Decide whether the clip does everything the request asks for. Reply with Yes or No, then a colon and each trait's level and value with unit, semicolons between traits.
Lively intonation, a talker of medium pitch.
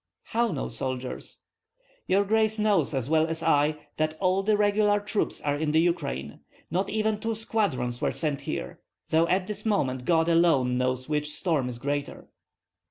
Yes: wide, 6.3 semitones; medium, 165 Hz